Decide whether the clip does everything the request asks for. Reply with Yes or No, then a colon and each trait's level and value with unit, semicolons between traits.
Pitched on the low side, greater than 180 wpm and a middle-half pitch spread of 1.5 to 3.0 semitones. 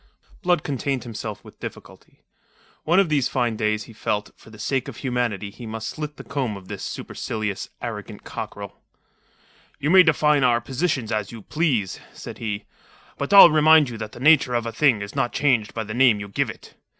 No: low, 120 Hz; average, 200 wpm; average, 5.3 semitones